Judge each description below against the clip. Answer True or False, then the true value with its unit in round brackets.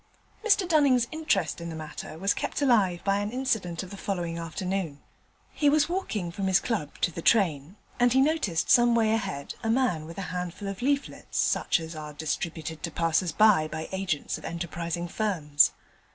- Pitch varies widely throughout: True (5.9 semitones)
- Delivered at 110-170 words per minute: False (185 wpm)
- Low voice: False (185 Hz)